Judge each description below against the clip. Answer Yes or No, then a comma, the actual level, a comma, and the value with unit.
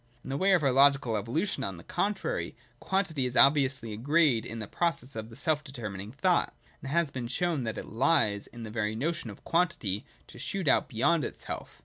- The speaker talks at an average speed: No, fast, 210 wpm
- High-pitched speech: No, low, 135 Hz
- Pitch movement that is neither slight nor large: No, wide, 6.5 semitones